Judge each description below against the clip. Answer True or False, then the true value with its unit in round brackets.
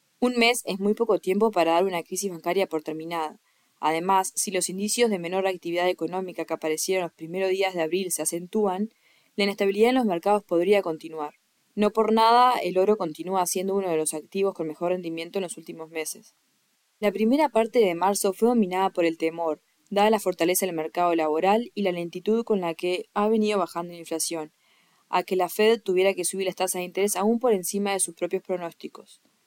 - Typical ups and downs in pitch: True (3.3 semitones)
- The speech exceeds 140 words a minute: True (205 wpm)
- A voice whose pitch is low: False (185 Hz)